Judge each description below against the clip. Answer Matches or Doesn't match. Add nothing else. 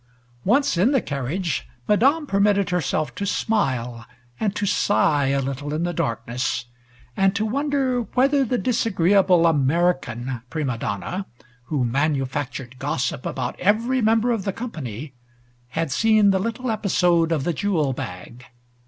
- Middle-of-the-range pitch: Matches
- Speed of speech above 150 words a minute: Doesn't match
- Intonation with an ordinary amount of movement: Doesn't match